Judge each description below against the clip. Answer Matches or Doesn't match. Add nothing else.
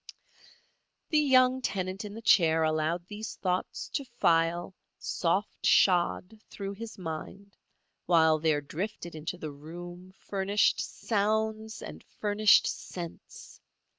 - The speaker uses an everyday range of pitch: Matches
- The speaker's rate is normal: Doesn't match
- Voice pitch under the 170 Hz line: Doesn't match